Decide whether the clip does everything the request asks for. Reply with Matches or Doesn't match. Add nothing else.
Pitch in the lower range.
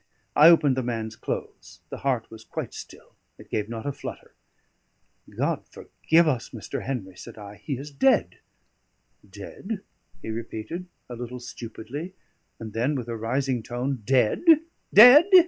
Matches